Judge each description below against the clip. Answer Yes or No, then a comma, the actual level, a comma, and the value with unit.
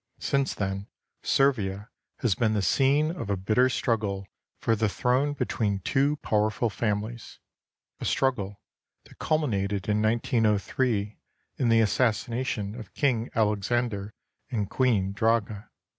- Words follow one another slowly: Yes, slow, 130 wpm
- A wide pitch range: No, average, 3.6 semitones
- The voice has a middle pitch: No, low, 110 Hz